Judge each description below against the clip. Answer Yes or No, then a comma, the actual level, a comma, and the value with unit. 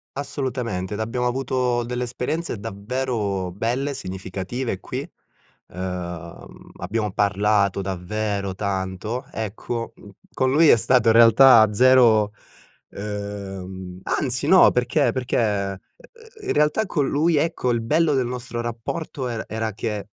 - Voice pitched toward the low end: Yes, low, 115 Hz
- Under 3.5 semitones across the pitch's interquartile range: No, average, 4.5 semitones